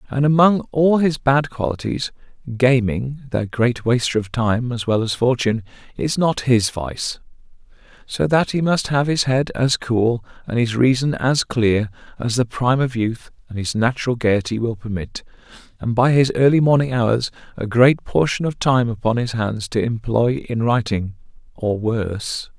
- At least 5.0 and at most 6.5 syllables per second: No, 4.5 syllables/s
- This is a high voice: No, low, 120 Hz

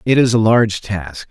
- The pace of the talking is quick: Yes, fast, 230 wpm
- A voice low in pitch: Yes, low, 110 Hz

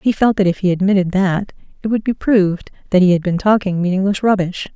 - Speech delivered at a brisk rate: Yes, fast, 225 wpm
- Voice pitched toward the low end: No, high, 190 Hz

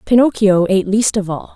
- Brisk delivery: No, average, 190 wpm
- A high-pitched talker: Yes, high, 205 Hz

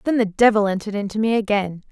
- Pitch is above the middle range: Yes, high, 210 Hz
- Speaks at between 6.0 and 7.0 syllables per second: Yes, 6.9 syllables/s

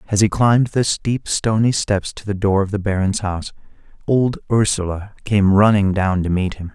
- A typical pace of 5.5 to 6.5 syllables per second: No, 4.9 syllables/s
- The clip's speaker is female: No, male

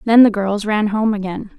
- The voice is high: Yes, high, 210 Hz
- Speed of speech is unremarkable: No, fast, 225 wpm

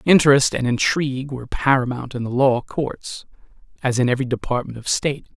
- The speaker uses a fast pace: No, average, 165 wpm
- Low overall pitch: Yes, low, 130 Hz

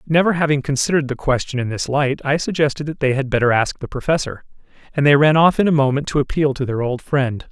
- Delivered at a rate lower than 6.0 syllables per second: No, 6.3 syllables/s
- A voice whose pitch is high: No, medium, 140 Hz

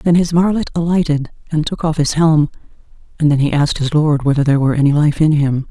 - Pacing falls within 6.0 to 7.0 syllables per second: Yes, 6.3 syllables/s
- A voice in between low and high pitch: Yes, medium, 150 Hz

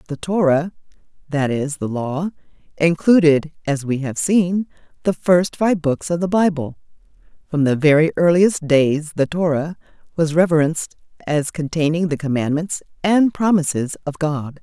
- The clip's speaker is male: No, female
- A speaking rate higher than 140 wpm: No, slow, 135 wpm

